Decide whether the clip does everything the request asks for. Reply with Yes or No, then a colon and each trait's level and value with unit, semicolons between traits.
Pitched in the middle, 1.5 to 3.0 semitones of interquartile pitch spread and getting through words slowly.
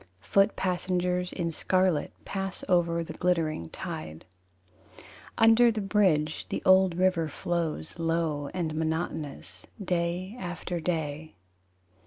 Yes: medium, 175 Hz; narrow, 2.6 semitones; slow, 110 wpm